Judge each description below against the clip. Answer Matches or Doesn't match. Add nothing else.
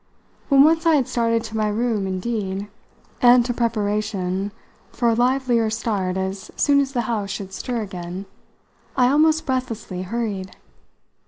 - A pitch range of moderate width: Matches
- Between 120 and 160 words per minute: Matches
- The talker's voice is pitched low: Doesn't match